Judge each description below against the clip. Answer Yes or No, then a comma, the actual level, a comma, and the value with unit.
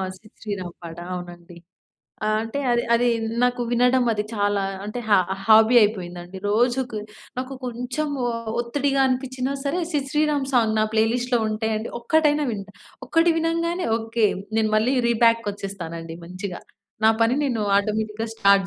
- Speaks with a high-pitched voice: Yes, high, 225 Hz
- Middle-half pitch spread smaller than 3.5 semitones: No, average, 3.9 semitones